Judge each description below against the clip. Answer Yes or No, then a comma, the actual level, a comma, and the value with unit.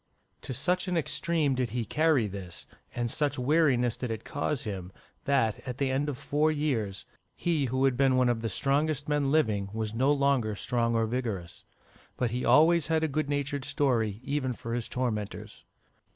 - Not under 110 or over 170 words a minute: No, average, 185 wpm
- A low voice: Yes, low, 130 Hz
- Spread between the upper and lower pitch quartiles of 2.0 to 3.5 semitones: No, average, 4.2 semitones